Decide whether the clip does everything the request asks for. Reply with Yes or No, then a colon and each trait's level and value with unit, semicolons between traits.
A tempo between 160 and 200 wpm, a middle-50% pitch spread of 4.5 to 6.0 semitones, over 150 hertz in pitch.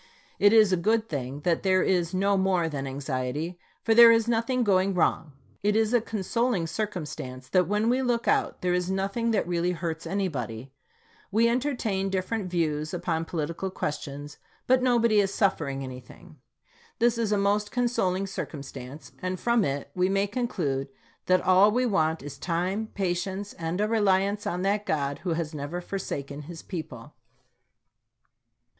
Yes: average, 165 wpm; average, 4.9 semitones; medium, 185 Hz